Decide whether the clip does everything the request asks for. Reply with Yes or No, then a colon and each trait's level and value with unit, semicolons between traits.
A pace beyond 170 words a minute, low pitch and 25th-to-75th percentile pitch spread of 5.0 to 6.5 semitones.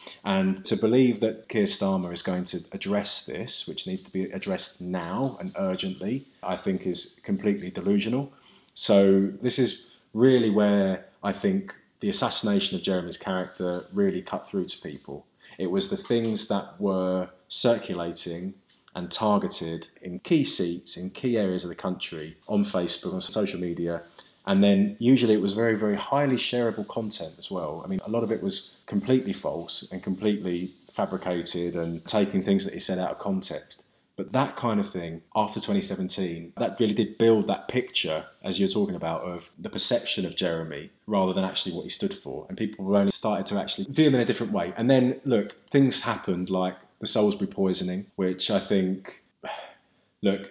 Yes: average, 180 wpm; low, 100 Hz; average, 5.3 semitones